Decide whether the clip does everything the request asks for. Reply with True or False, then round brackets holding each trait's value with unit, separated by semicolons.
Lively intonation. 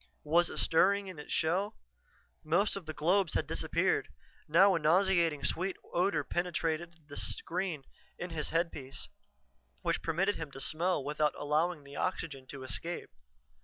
False (3.3 semitones)